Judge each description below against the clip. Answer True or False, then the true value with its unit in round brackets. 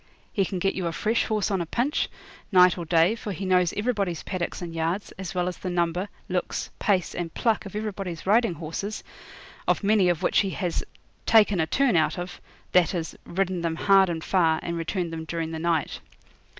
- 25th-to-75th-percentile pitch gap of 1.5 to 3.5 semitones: True (2.9 semitones)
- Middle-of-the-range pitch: True (180 Hz)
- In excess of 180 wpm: True (205 wpm)